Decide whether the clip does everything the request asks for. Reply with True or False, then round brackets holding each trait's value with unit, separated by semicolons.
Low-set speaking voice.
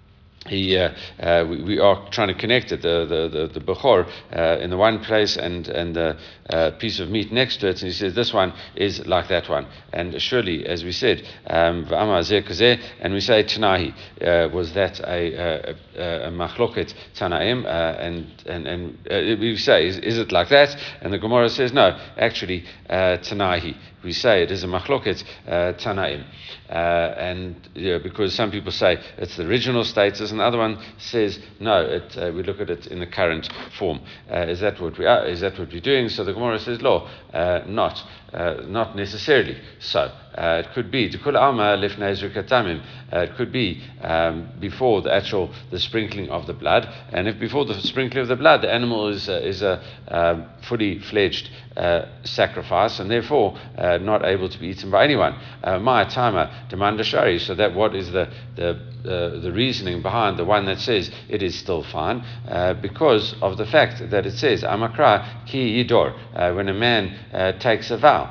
True (100 Hz)